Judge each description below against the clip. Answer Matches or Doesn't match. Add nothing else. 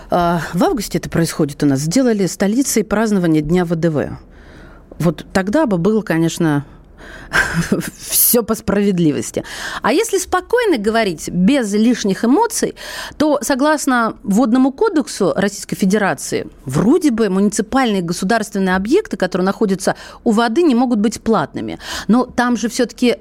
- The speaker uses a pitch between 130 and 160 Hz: Doesn't match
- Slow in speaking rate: Doesn't match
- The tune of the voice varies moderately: Doesn't match